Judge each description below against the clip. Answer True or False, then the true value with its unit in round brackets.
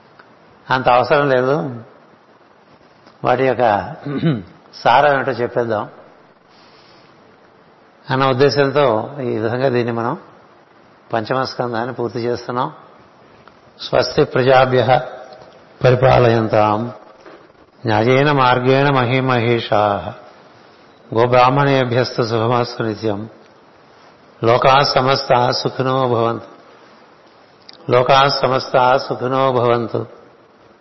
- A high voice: False (125 Hz)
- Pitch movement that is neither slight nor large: False (2.2 semitones)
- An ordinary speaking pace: False (65 wpm)